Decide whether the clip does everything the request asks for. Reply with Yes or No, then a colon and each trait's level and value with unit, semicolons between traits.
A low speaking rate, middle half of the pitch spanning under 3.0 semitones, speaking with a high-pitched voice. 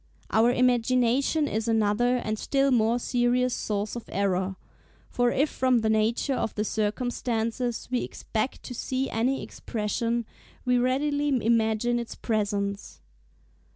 Yes: slow, 130 wpm; narrow, 2.5 semitones; high, 235 Hz